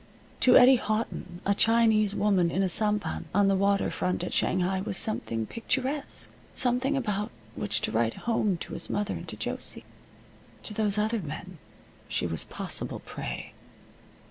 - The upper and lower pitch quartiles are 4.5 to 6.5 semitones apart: No, average, 3.6 semitones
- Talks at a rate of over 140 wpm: Yes, average, 160 wpm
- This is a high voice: Yes, high, 205 Hz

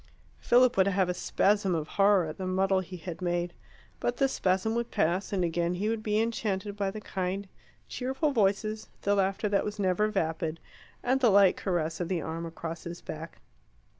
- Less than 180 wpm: No, average, 195 wpm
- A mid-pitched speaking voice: No, high, 195 Hz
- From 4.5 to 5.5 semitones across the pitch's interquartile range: No, average, 3.3 semitones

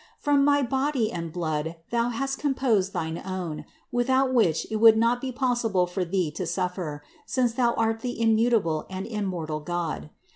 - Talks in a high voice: Yes, high, 220 Hz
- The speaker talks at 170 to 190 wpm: Yes, average, 175 wpm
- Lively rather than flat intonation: Yes, wide, 5.9 semitones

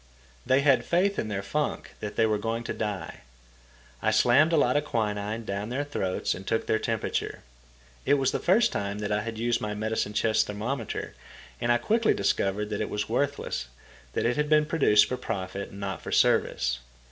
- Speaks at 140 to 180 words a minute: No, average, 195 wpm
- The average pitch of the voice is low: Yes, low, 110 Hz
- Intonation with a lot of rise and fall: No, average, 4.7 semitones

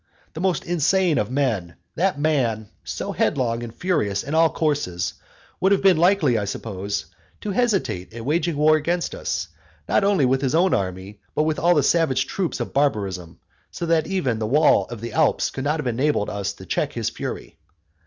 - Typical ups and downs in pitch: No, wide, 7.4 semitones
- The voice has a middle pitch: Yes, medium, 145 Hz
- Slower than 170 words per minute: No, average, 195 wpm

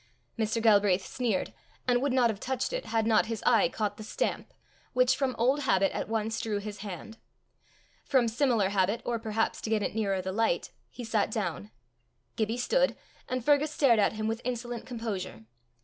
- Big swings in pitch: No, average, 3.0 semitones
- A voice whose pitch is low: No, high, 225 Hz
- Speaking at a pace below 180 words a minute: No, average, 185 wpm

